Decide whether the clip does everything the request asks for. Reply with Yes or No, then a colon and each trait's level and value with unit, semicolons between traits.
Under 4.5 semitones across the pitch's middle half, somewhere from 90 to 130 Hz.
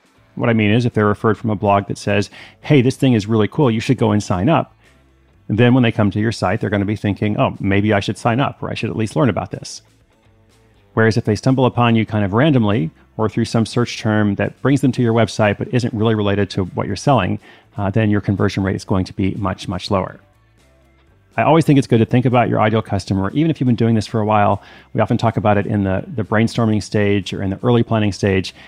Yes: average, 2.7 semitones; low, 110 Hz